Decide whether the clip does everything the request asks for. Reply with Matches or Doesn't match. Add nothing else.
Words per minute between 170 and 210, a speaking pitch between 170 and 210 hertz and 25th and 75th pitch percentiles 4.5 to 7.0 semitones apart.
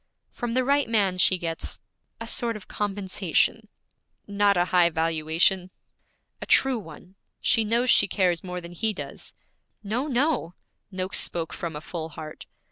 Doesn't match